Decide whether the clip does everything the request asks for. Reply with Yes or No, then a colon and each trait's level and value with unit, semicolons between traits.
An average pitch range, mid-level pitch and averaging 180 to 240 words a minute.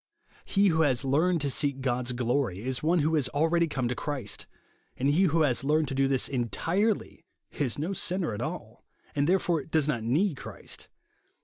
Yes: average, 4.0 semitones; medium, 145 Hz; average, 190 wpm